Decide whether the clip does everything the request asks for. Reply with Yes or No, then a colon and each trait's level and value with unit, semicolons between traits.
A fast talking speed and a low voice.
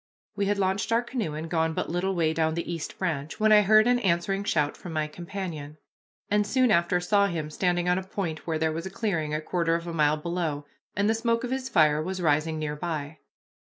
No: fast, 235 wpm; medium, 170 Hz